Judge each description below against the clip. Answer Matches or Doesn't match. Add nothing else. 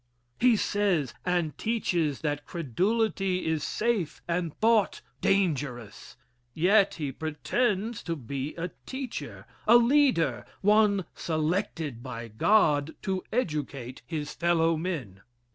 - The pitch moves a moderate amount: Doesn't match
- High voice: Doesn't match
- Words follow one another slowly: Matches